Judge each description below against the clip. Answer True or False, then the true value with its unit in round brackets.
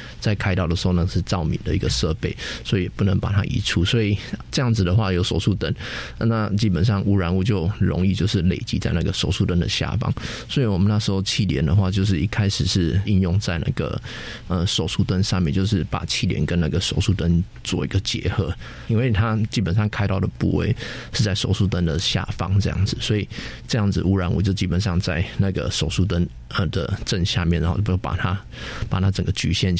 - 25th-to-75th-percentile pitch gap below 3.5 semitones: True (2.9 semitones)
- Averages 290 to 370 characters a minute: True (320 characters per minute)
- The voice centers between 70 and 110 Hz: True (95 Hz)